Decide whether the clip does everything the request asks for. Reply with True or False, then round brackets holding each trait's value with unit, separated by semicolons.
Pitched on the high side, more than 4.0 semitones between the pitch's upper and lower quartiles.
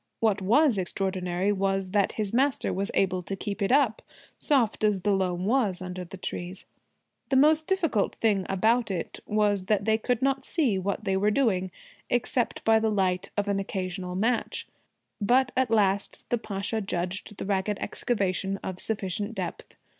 False (205 Hz; 3.1 semitones)